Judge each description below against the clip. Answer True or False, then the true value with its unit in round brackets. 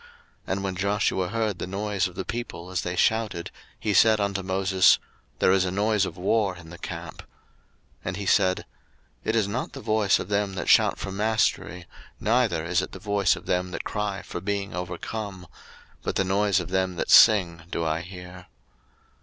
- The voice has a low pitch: True (95 Hz)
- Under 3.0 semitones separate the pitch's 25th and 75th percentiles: True (2.4 semitones)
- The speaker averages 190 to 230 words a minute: True (195 wpm)